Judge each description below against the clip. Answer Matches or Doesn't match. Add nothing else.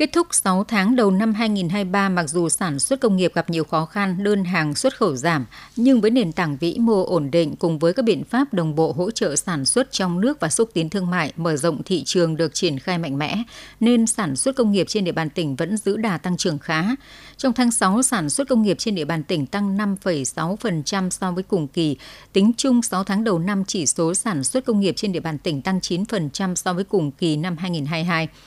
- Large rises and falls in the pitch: Doesn't match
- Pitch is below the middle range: Doesn't match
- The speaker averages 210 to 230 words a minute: Doesn't match